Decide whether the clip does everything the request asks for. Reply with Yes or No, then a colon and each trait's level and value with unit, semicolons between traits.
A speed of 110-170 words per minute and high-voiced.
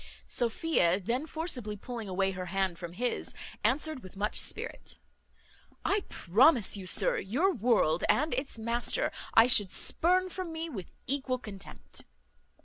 Yes: average, 140 wpm; high, 235 Hz